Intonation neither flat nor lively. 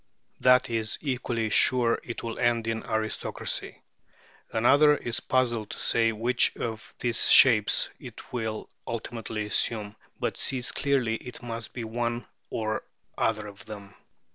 No: narrow, 1.8 semitones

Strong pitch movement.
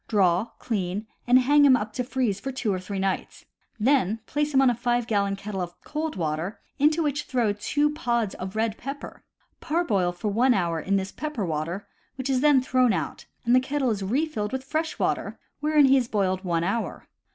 Yes: wide, 5.7 semitones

